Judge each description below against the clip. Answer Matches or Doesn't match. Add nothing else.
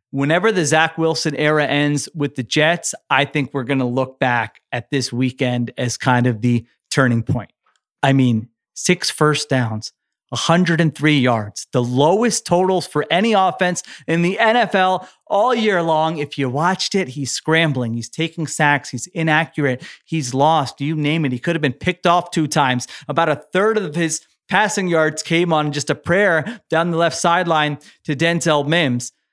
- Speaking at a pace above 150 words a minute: Matches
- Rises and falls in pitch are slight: Doesn't match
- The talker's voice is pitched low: Doesn't match